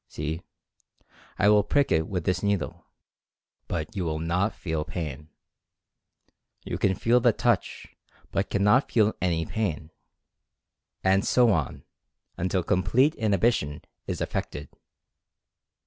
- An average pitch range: Yes, average, 4.5 semitones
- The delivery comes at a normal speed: No, slow, 120 wpm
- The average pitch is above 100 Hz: No, very low, 95 Hz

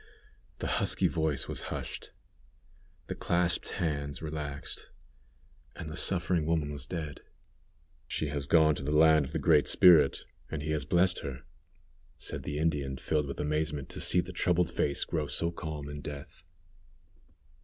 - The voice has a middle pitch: No, very low, 75 Hz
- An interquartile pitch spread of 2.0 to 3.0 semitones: Yes, narrow, 2.4 semitones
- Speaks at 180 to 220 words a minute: No, average, 155 wpm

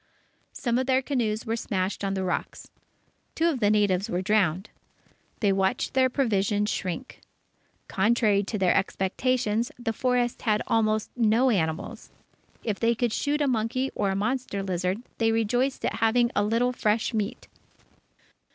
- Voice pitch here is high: Yes, high, 220 Hz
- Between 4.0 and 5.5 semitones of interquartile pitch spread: No, average, 3.6 semitones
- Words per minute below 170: Yes, average, 155 wpm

